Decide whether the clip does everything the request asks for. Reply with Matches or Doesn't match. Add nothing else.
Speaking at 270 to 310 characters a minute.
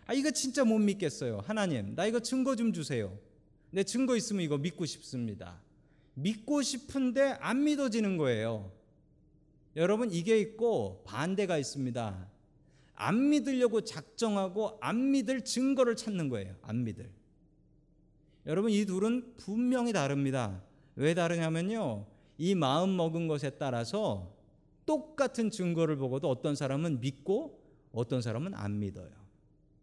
Matches